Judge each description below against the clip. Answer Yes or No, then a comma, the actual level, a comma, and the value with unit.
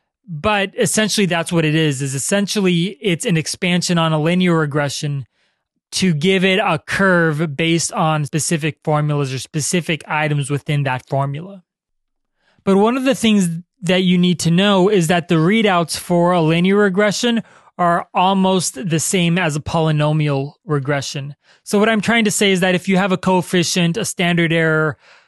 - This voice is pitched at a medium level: Yes, medium, 175 Hz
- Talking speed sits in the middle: Yes, average, 170 wpm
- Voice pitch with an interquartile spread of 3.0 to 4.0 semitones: Yes, average, 3.7 semitones